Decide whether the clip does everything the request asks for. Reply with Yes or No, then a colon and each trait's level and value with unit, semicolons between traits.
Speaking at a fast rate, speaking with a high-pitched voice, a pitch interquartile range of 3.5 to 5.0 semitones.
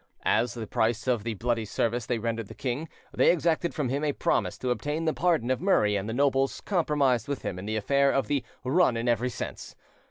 No: fast, 225 wpm; low, 125 Hz; average, 4.0 semitones